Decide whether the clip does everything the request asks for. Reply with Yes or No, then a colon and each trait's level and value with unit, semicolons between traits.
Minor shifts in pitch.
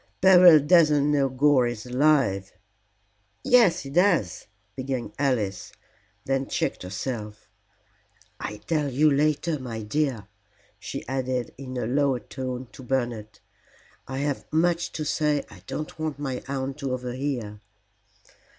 No: average, 3.4 semitones